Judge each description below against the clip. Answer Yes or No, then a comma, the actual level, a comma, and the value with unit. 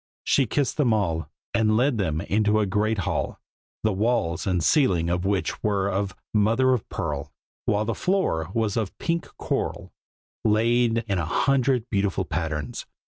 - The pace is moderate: Yes, average, 160 wpm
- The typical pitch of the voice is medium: No, low, 105 Hz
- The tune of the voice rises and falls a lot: No, average, 3.9 semitones